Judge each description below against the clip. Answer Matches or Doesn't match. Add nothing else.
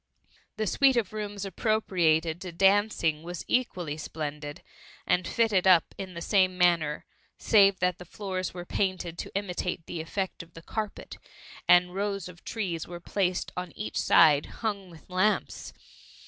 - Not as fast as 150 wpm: Doesn't match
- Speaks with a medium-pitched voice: Matches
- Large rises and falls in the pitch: Doesn't match